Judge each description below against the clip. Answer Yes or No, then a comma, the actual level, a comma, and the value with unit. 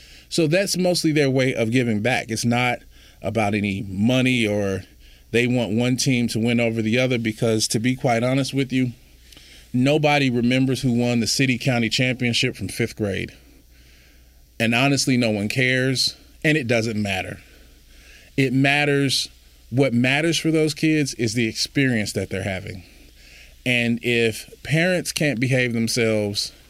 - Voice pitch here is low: Yes, low, 120 Hz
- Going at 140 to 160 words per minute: Yes, average, 155 wpm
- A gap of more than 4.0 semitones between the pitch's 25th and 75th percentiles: Yes, average, 4.5 semitones